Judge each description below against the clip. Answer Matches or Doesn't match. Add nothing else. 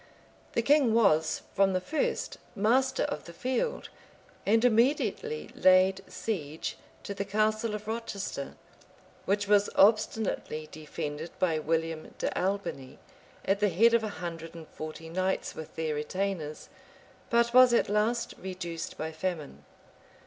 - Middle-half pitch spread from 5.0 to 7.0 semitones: Matches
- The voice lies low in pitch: Doesn't match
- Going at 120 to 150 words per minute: Matches